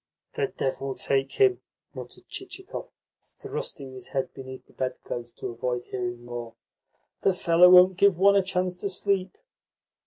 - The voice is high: No, medium, 180 Hz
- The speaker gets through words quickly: No, average, 150 wpm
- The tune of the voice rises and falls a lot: Yes, wide, 7.5 semitones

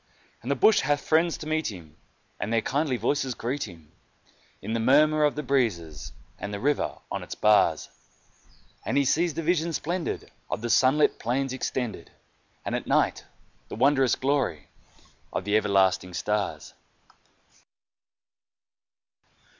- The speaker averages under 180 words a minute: Yes, average, 145 wpm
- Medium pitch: No, low, 130 Hz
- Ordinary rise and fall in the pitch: No, wide, 6.0 semitones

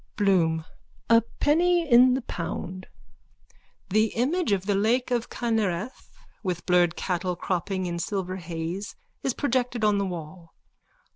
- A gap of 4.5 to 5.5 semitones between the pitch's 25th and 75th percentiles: Yes, average, 5.1 semitones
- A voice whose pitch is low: No, high, 200 Hz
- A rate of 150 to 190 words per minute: No, slow, 135 wpm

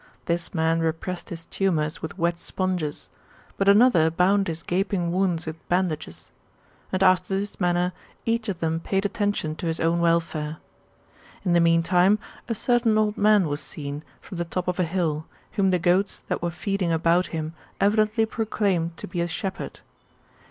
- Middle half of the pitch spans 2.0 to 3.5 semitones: Yes, average, 3.0 semitones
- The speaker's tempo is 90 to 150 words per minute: No, average, 170 wpm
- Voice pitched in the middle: Yes, medium, 175 Hz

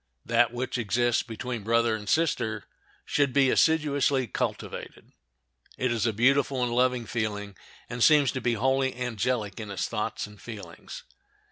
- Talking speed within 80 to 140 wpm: No, average, 150 wpm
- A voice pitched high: No, low, 120 Hz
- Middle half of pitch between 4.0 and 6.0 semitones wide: No, average, 2.9 semitones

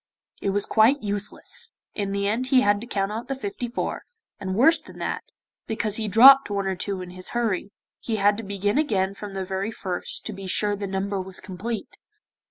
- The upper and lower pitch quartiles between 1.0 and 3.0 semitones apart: Yes, average, 2.7 semitones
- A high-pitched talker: Yes, high, 205 Hz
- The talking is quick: Yes, fast, 210 wpm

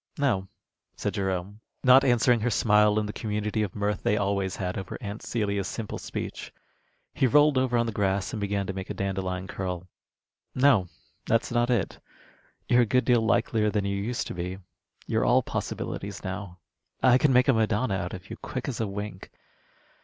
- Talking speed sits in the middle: Yes, average, 190 wpm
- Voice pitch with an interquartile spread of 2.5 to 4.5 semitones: Yes, average, 3.6 semitones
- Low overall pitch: Yes, low, 105 Hz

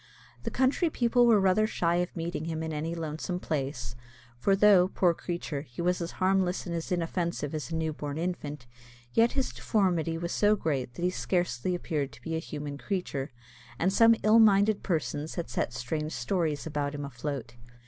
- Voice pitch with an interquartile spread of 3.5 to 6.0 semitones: Yes, average, 4.1 semitones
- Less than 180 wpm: No, average, 185 wpm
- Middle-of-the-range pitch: Yes, medium, 170 Hz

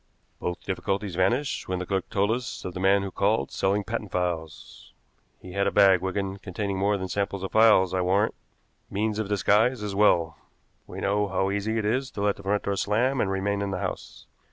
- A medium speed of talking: No, fast, 210 wpm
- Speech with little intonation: Yes, narrow, 1.7 semitones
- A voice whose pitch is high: No, low, 100 Hz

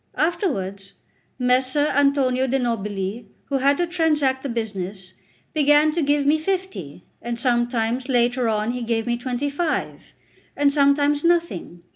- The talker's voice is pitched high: Yes, very high, 260 Hz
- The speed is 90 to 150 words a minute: Yes, average, 140 wpm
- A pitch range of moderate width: Yes, average, 4.1 semitones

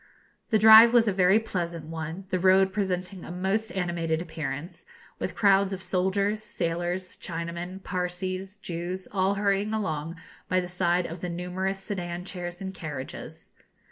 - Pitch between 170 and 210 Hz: Yes, medium, 185 Hz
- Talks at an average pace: Yes, average, 150 wpm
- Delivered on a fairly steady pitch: Yes, narrow, 2.0 semitones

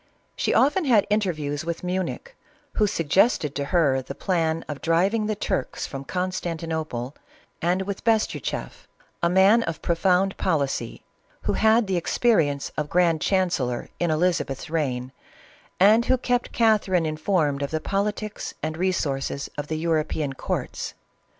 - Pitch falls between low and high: Yes, medium, 170 Hz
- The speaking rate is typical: Yes, average, 150 wpm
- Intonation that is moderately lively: Yes, average, 4.7 semitones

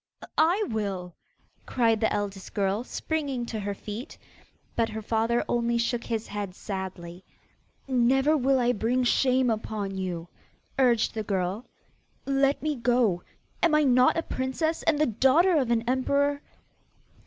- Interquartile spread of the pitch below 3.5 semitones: No, average, 4.5 semitones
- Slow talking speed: No, average, 145 wpm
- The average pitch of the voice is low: No, high, 235 Hz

